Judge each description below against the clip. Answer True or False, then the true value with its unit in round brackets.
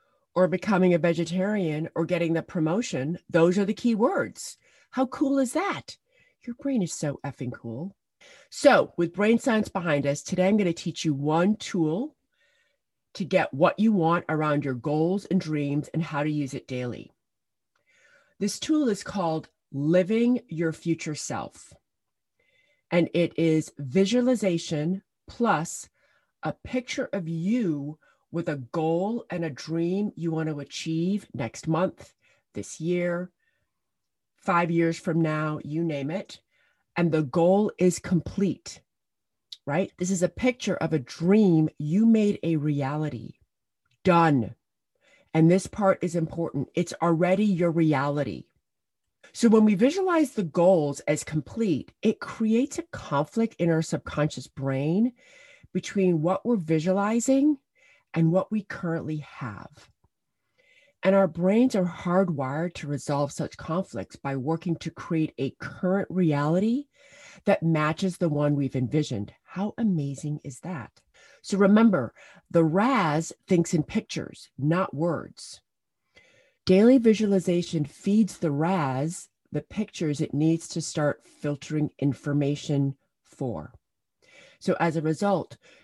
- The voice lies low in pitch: False (170 Hz)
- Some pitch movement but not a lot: True (4.7 semitones)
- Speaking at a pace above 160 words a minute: False (135 wpm)